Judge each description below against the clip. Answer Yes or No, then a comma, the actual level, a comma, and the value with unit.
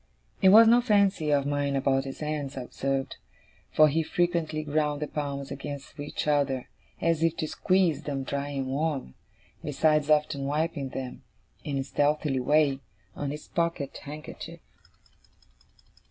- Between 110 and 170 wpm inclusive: Yes, average, 150 wpm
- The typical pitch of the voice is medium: Yes, medium, 145 Hz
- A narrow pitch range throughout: Yes, narrow, 2.2 semitones